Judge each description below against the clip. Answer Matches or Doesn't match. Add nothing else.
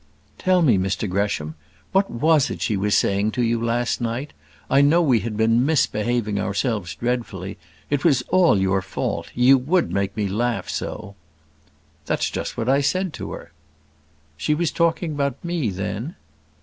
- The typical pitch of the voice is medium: Doesn't match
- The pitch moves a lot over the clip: Matches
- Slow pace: Doesn't match